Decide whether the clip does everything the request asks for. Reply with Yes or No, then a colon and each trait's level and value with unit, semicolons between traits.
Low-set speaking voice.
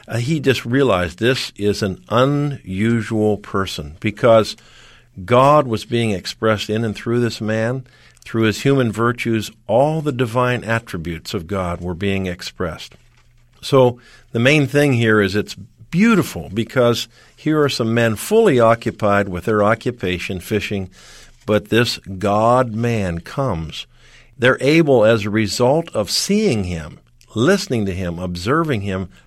Yes: low, 115 Hz